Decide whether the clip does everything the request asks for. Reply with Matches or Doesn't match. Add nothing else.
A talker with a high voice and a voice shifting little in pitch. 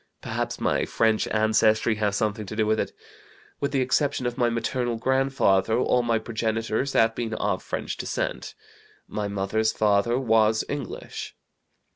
Doesn't match